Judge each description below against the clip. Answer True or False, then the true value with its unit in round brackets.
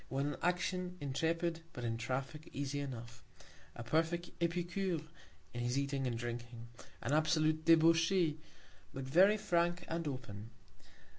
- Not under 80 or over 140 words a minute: True (135 wpm)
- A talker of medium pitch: True (155 Hz)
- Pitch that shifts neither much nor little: True (4.9 semitones)